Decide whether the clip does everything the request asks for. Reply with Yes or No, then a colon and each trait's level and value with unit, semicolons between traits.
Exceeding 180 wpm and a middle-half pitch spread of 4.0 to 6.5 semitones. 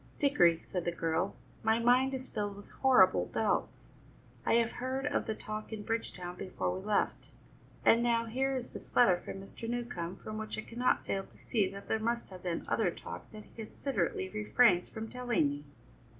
Yes: average, 195 wpm; average, 4.4 semitones